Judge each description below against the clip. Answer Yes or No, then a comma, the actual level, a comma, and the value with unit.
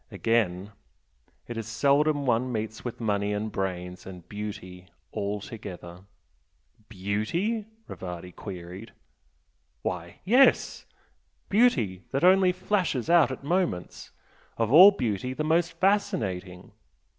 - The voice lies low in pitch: Yes, low, 110 Hz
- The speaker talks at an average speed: No, slow, 110 wpm